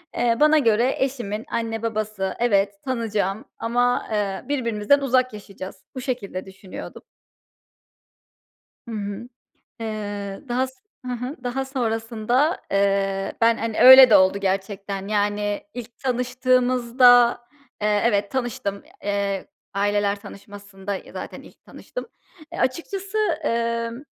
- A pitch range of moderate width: Yes, average, 3.6 semitones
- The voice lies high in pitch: Yes, high, 225 Hz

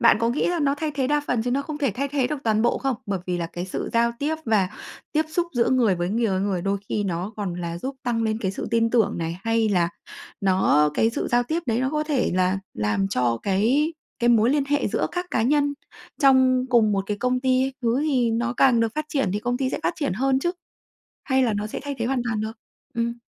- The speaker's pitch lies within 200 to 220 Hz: No, high, 235 Hz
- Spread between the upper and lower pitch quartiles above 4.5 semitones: Yes, average, 5.1 semitones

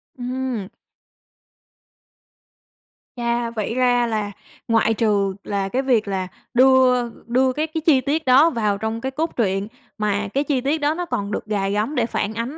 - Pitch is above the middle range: Yes, high, 235 Hz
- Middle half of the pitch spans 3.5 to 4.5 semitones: Yes, average, 3.9 semitones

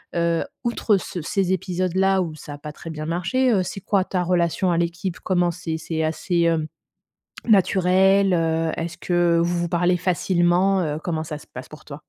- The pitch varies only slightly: Yes, narrow, 2.1 semitones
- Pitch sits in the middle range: Yes, medium, 175 Hz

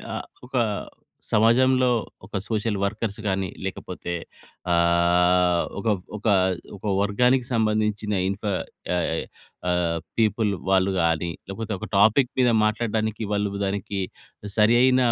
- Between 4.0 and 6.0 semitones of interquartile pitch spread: No, average, 3.0 semitones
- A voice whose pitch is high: No, low, 105 Hz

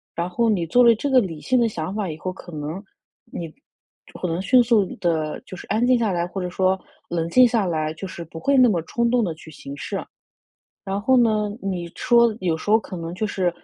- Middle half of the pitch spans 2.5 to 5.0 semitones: No, wide, 5.4 semitones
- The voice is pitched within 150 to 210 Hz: Yes, high, 190 Hz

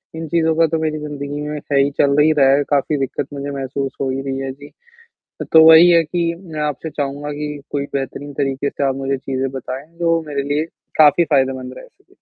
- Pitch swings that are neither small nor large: No, narrow, 2.1 semitones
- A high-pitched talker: No, medium, 145 Hz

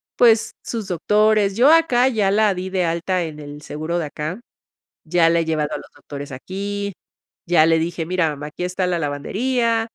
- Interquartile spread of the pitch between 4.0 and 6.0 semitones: Yes, average, 4.8 semitones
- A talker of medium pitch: Yes, medium, 180 Hz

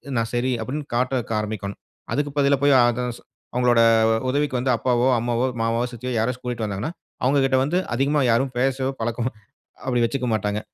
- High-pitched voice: No, low, 125 Hz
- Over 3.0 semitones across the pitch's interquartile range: No, narrow, 2.5 semitones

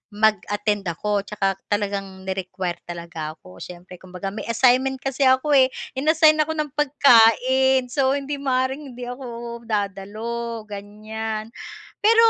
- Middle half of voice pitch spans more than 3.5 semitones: Yes, average, 5.0 semitones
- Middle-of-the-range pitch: No, high, 230 Hz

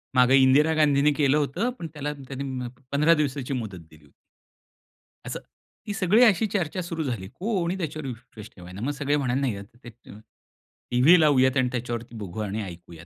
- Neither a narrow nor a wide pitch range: Yes, average, 4.6 semitones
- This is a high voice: No, low, 135 Hz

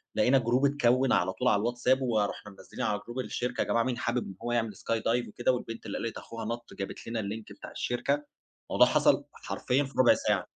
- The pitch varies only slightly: Yes, narrow, 2.1 semitones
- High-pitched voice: No, low, 120 Hz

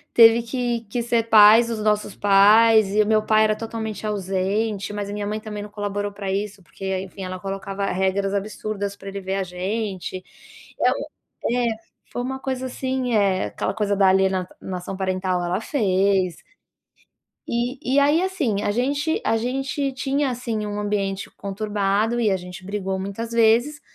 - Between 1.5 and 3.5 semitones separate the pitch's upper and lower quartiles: Yes, average, 2.9 semitones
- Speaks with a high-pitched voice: Yes, high, 210 Hz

